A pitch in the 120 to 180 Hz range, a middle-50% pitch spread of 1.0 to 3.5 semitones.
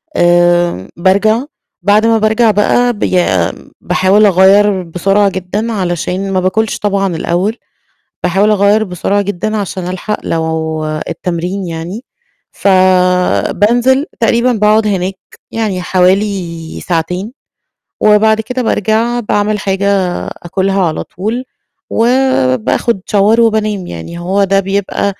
No: high, 195 Hz; average, 3.1 semitones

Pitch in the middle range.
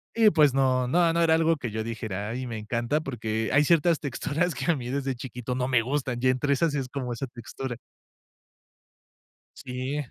No: low, 130 Hz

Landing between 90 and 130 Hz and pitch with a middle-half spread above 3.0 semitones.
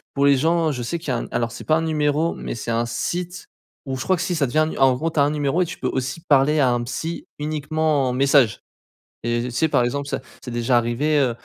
No: medium, 140 Hz; average, 3.9 semitones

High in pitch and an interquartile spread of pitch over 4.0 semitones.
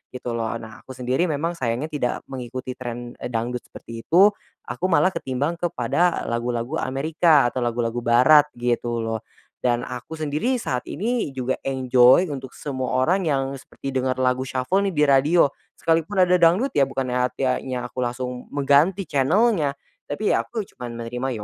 No: low, 130 Hz; average, 4.6 semitones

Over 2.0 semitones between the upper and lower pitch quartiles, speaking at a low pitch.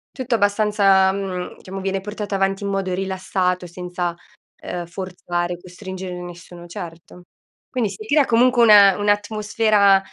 No: narrow, 2.4 semitones; high, 195 Hz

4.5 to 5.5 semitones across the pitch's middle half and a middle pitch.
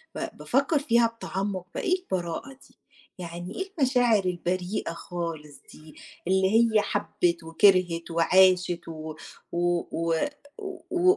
Yes: average, 5.2 semitones; medium, 180 Hz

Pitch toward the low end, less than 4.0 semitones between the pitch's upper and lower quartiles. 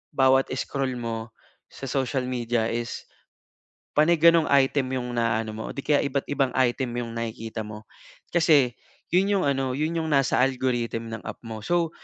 Yes: low, 130 Hz; average, 3.3 semitones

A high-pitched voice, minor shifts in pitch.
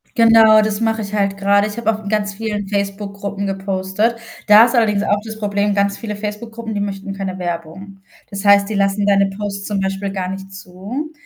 Yes: high, 200 Hz; narrow, 1.5 semitones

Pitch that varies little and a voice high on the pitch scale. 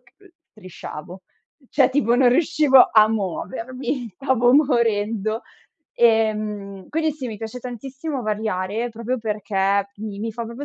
No: average, 3.5 semitones; high, 225 Hz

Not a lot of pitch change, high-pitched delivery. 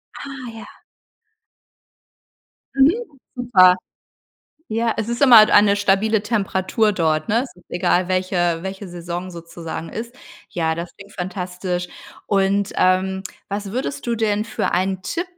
No: average, 3.8 semitones; high, 195 Hz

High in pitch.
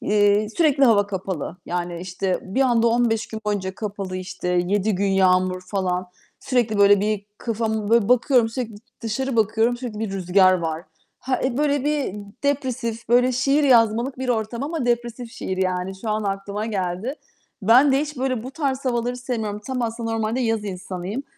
Yes: high, 220 Hz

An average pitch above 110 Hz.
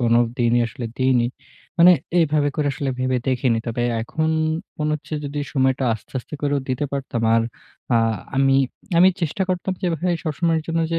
Yes: medium, 140 Hz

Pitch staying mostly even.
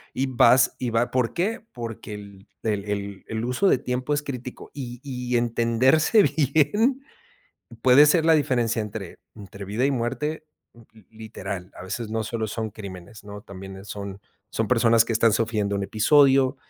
No: average, 4.1 semitones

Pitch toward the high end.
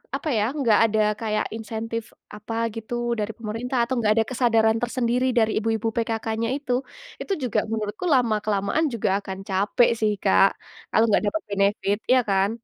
Yes: high, 225 Hz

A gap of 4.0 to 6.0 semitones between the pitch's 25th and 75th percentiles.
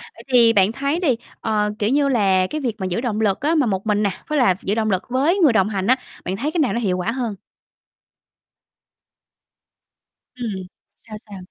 Yes: average, 4.9 semitones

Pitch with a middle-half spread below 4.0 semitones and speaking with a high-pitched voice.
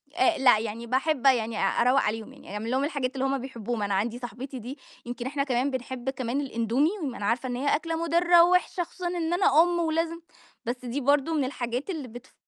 No: average, 4.6 semitones; very high, 265 Hz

